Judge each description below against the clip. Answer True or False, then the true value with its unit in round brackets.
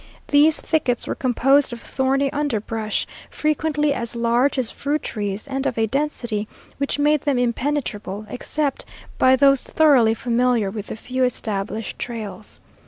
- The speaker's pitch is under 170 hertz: False (250 Hz)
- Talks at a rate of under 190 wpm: True (145 wpm)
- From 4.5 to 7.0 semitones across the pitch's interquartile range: False (4.1 semitones)